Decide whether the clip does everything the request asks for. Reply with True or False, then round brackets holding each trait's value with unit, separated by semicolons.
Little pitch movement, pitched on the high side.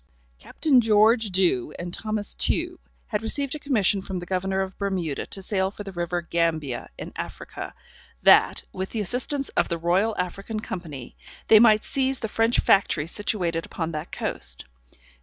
False (4.2 semitones; 195 Hz)